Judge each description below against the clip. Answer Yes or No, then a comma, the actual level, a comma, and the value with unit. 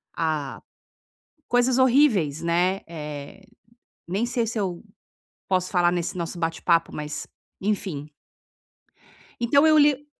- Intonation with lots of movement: Yes, wide, 6.4 semitones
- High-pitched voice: No, medium, 180 Hz